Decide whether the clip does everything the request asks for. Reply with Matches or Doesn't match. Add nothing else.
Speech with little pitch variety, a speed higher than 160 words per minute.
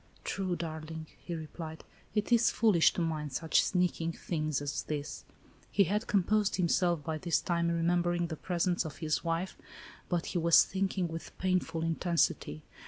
Matches